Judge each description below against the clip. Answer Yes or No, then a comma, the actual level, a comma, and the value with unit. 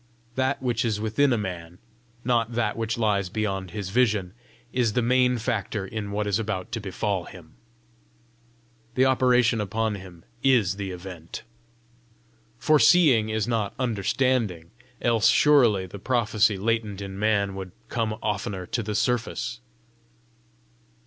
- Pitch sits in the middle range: No, low, 110 Hz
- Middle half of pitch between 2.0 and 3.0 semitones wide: No, average, 3.5 semitones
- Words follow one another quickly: No, slow, 135 wpm